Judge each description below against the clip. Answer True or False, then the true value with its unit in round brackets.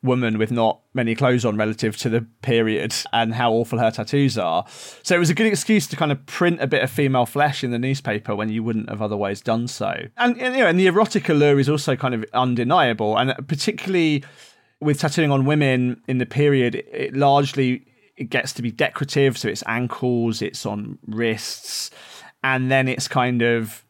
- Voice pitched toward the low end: True (125 Hz)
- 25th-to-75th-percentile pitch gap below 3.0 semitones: False (3.7 semitones)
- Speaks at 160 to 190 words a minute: False (205 wpm)